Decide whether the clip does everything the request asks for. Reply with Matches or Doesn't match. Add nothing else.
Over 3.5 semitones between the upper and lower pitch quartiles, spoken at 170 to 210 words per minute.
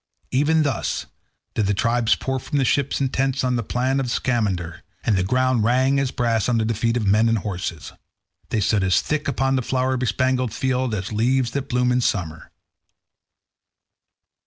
Doesn't match